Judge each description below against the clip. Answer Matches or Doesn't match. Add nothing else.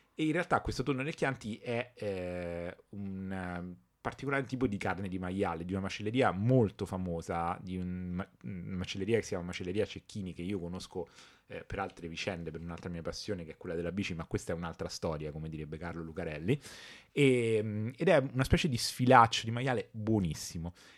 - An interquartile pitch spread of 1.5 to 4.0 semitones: Doesn't match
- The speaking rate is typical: Doesn't match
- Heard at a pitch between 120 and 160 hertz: Doesn't match